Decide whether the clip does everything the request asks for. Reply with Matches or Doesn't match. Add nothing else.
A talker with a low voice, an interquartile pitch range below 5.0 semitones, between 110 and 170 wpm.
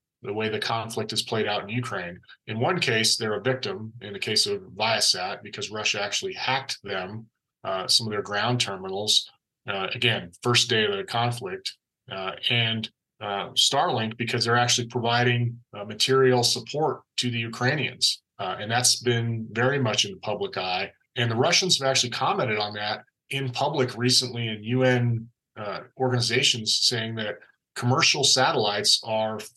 Matches